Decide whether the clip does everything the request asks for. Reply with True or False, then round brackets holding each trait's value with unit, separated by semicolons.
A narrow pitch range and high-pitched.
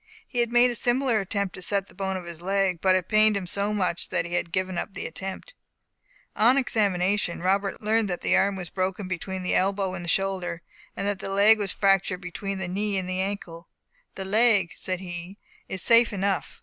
True (2.0 semitones; 195 Hz)